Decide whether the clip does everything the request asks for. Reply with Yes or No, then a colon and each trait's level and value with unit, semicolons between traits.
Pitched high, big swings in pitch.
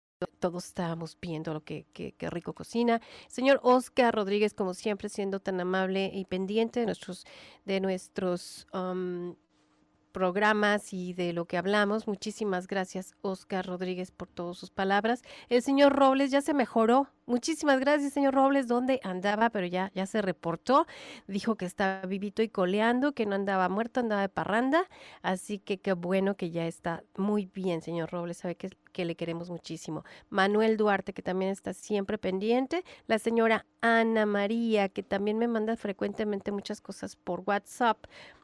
No: high, 200 Hz; average, 3.8 semitones